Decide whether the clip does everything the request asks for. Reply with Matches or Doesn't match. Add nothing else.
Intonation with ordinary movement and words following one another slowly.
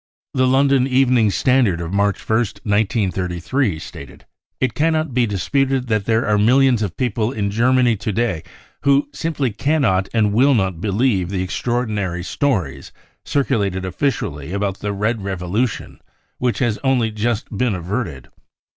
Doesn't match